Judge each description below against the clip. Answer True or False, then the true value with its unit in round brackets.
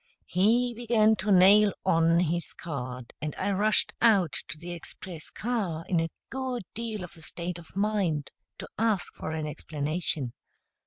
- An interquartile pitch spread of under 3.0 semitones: False (4.9 semitones)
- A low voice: False (180 Hz)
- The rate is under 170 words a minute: True (160 wpm)